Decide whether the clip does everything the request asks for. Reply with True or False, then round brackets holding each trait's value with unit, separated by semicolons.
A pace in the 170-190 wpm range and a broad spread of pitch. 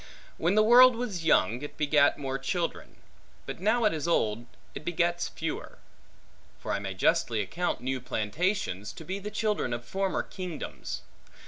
False (160 wpm; 7.7 semitones)